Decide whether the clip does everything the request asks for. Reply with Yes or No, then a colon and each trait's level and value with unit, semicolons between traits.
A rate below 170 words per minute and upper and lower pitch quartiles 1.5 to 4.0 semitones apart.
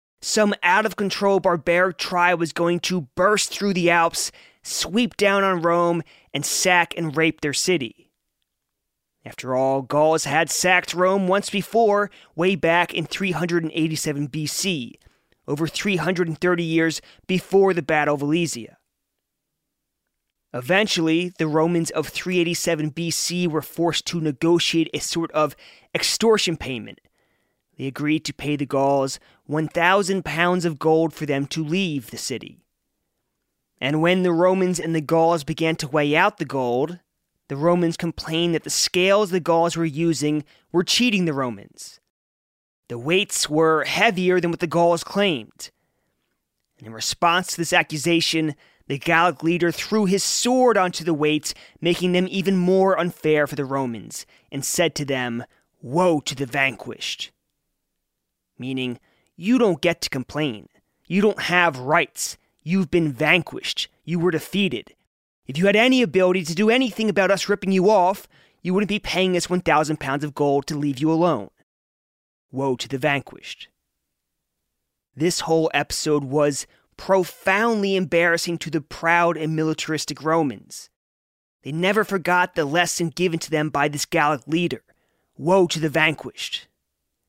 Yes: average, 150 wpm; average, 3.3 semitones